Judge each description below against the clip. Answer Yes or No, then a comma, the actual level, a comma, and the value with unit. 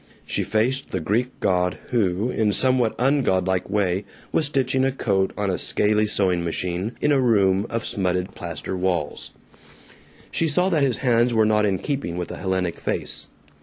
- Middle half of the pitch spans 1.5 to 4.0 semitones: No, average, 5.3 semitones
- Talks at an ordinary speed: Yes, average, 175 wpm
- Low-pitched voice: Yes, low, 105 Hz